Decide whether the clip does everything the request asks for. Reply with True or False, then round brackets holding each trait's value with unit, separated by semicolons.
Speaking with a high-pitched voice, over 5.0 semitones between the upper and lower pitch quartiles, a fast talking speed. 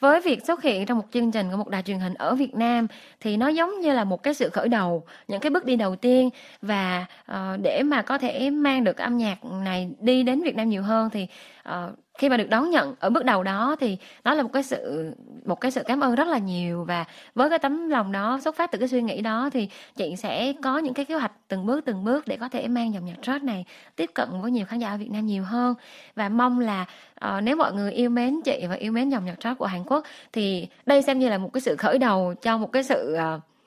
True (245 Hz; 5.4 semitones; 275 wpm)